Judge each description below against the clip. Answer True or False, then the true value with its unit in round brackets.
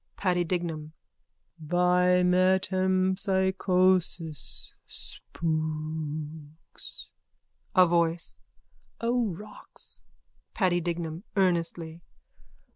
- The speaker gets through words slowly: True (55 wpm)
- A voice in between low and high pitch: True (175 Hz)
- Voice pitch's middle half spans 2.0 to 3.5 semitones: True (2.5 semitones)